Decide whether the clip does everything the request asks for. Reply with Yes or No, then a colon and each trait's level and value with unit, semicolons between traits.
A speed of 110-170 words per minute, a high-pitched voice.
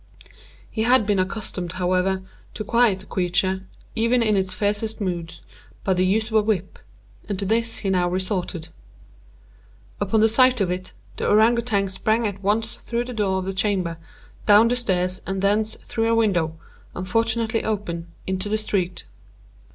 Yes: average, 165 wpm; high, 200 Hz